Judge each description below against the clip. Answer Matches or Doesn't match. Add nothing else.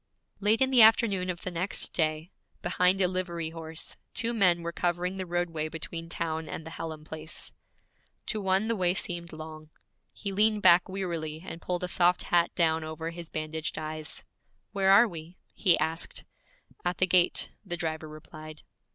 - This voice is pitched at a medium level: Matches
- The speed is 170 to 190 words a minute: Matches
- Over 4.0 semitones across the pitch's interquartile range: Doesn't match